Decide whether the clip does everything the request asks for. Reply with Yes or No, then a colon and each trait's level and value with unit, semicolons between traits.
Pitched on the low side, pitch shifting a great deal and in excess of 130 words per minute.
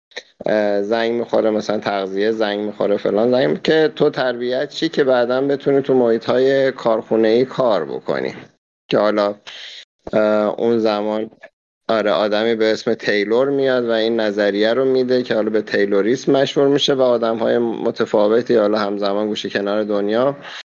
No: low, 110 Hz; average, 3.2 semitones; average, 150 wpm